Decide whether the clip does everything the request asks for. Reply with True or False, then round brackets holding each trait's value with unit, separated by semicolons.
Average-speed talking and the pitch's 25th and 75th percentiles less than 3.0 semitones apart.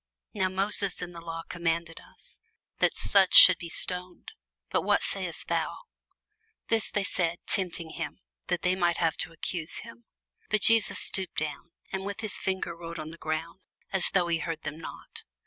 True (180 wpm; 2.4 semitones)